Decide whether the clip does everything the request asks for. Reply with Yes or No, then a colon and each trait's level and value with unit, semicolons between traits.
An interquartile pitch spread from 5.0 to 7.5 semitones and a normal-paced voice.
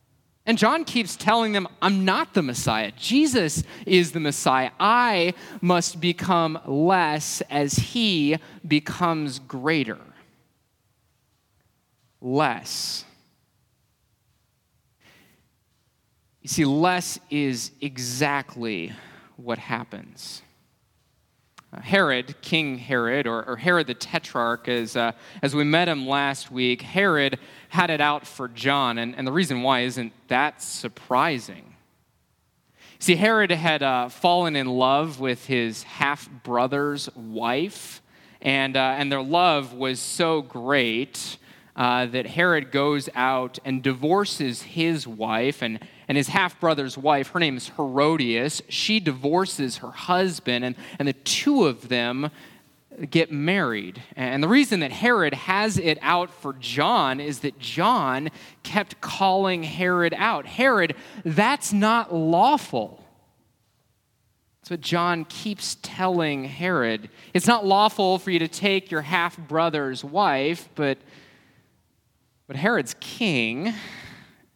No: wide, 5.6 semitones; slow, 120 wpm